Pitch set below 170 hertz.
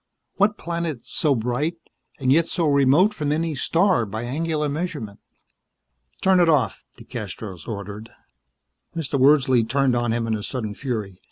Yes: low, 135 Hz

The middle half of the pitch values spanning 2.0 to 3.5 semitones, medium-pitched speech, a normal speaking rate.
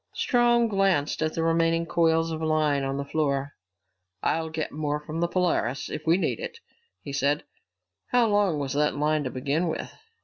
Yes: average, 2.7 semitones; medium, 155 Hz; average, 180 wpm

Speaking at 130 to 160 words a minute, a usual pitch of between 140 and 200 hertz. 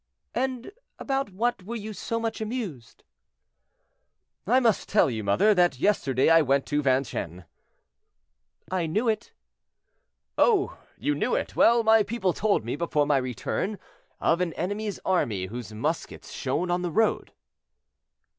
Yes: average, 145 wpm; medium, 185 Hz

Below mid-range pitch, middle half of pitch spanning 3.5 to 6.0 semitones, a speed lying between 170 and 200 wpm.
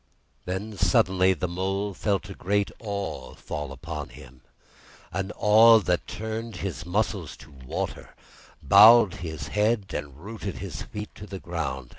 No: very low, 95 Hz; average, 3.9 semitones; average, 145 wpm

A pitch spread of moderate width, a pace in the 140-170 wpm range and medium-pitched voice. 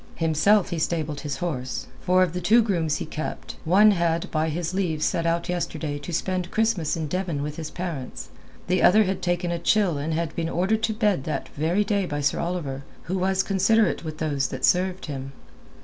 No: average, 3.3 semitones; fast, 205 wpm; medium, 170 Hz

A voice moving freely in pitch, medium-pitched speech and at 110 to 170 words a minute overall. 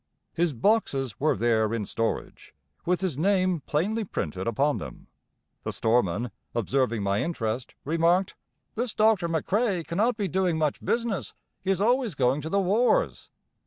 Yes: wide, 8.4 semitones; medium, 165 Hz; average, 150 wpm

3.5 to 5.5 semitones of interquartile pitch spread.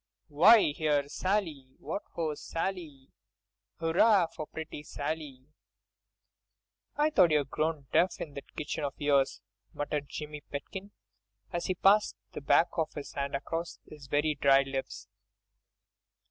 No: average, 3.0 semitones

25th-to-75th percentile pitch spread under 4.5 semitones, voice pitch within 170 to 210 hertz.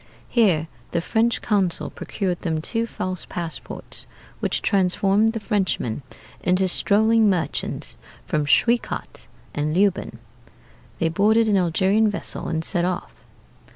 Yes: average, 4.1 semitones; high, 190 Hz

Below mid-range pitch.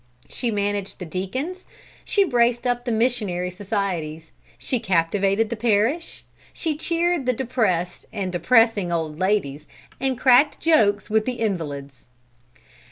No: high, 215 Hz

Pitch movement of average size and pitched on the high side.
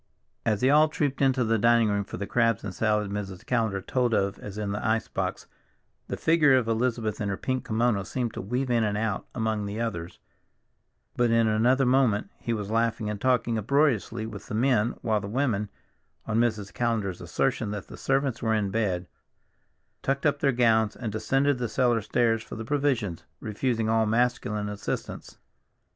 No: average, 3.0 semitones; low, 115 Hz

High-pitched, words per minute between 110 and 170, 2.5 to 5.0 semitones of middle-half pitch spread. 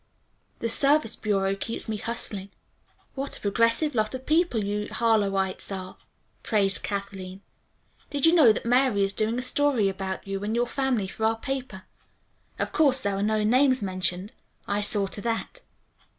Yes: high, 215 Hz; average, 165 wpm; average, 4.3 semitones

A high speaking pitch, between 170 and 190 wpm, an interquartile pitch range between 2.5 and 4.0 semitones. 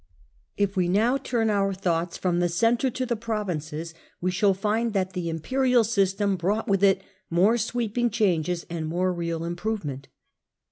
No: high, 195 Hz; average, 175 wpm; average, 4.4 semitones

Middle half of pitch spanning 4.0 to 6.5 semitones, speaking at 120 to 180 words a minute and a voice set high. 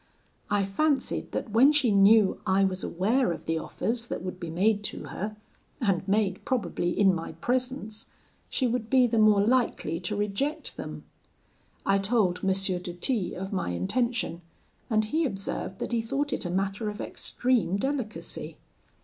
Yes: average, 4.3 semitones; average, 165 wpm; high, 210 Hz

